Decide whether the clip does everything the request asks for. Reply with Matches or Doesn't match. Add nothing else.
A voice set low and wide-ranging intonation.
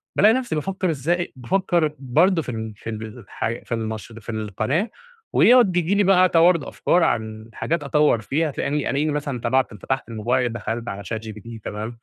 Matches